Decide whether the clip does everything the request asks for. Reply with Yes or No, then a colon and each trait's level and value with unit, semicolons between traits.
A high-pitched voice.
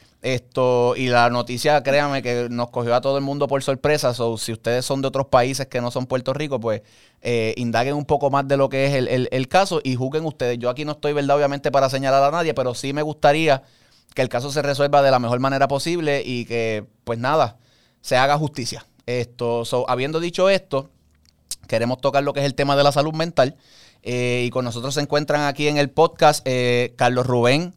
No: low, 135 Hz